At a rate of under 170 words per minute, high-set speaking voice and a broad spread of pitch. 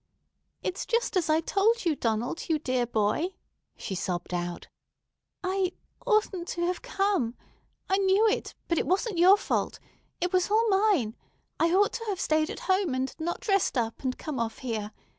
No: average, 175 wpm; very high, 345 Hz; wide, 7.5 semitones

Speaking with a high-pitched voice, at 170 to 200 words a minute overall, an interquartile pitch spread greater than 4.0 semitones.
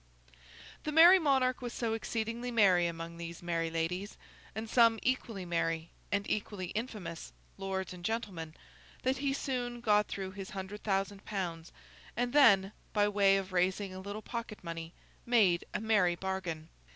No: high, 200 Hz; average, 155 wpm; average, 4.5 semitones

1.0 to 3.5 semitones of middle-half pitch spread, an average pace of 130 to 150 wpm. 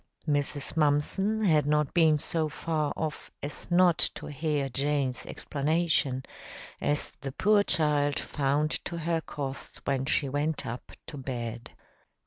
Yes: narrow, 2.5 semitones; slow, 135 wpm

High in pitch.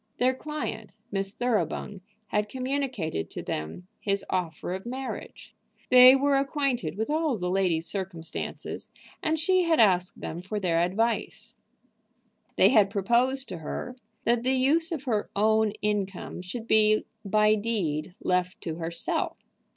Yes: high, 215 Hz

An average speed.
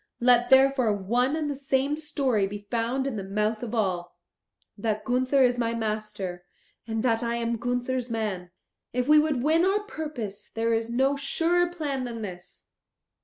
Yes: average, 170 wpm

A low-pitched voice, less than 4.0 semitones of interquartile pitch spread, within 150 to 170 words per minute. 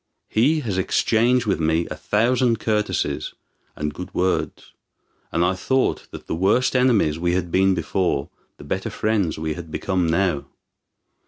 No: very low, 95 Hz; average, 5.1 semitones; average, 155 wpm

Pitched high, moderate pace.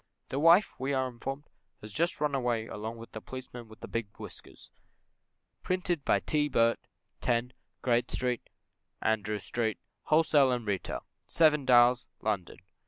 No: low, 125 Hz; average, 150 wpm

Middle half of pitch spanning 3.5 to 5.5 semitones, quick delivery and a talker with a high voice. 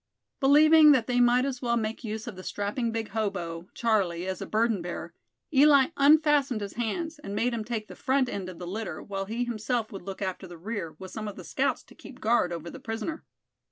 Yes: average, 4.4 semitones; fast, 225 wpm; high, 225 Hz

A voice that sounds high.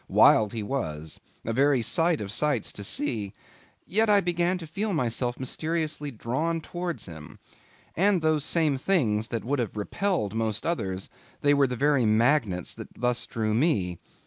No: low, 135 Hz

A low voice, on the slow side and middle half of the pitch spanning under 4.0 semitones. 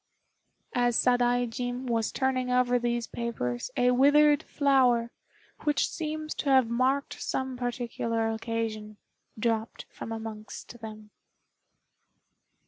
No: high, 245 Hz; slow, 105 wpm; narrow, 2.4 semitones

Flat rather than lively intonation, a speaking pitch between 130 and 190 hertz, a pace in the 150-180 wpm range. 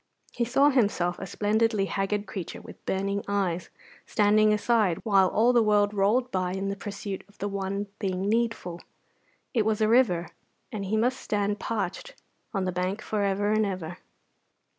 No: narrow, 2.1 semitones; high, 205 Hz; average, 165 wpm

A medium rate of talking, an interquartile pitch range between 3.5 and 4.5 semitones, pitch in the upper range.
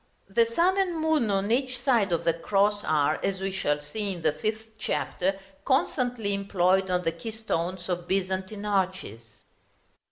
Yes: average, 160 wpm; average, 3.8 semitones; high, 195 Hz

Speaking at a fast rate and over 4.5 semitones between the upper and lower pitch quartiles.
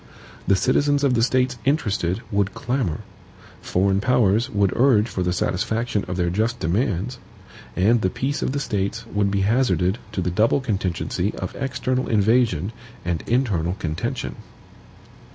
No: average, 150 wpm; average, 4.9 semitones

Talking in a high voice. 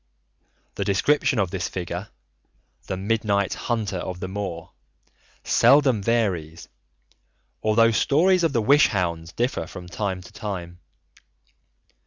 No: low, 100 Hz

